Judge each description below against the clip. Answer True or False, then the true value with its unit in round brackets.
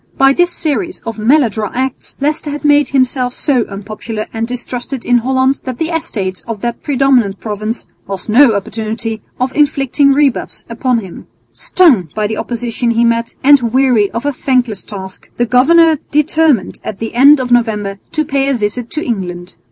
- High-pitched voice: True (245 Hz)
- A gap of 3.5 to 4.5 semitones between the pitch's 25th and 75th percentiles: True (4.1 semitones)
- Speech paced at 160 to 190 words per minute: True (175 wpm)